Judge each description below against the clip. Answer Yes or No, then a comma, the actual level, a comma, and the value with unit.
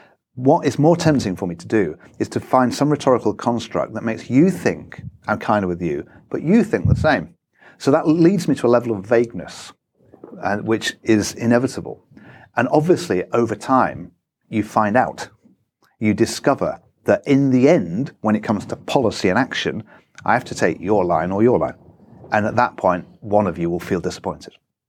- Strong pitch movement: No, average, 4.2 semitones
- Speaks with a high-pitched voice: No, low, 115 Hz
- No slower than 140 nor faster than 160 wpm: No, average, 195 wpm